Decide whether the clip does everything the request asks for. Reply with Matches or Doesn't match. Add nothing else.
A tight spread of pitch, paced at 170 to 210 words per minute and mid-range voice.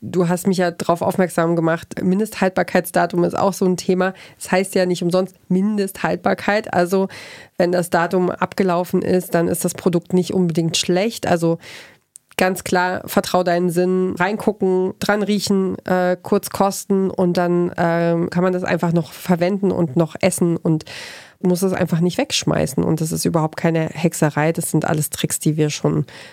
Matches